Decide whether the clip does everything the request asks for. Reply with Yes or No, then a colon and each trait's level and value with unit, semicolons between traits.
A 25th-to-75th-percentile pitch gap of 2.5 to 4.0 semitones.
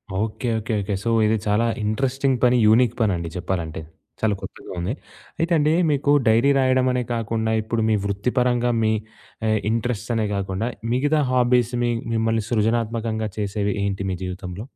Yes: average, 3.0 semitones